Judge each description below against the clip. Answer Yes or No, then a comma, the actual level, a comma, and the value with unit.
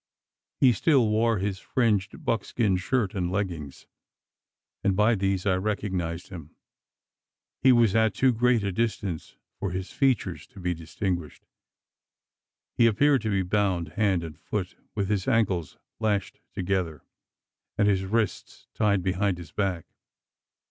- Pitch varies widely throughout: No, average, 3.3 semitones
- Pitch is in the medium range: No, low, 100 Hz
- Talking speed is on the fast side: No, average, 140 wpm